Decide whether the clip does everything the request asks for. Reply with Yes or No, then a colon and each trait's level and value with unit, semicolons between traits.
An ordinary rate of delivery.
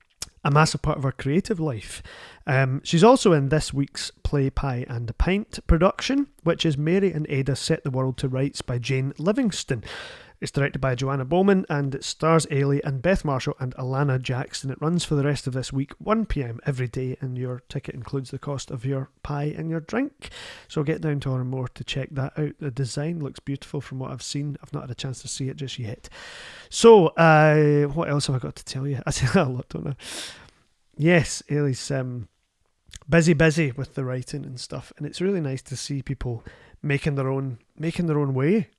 No: fast, 215 wpm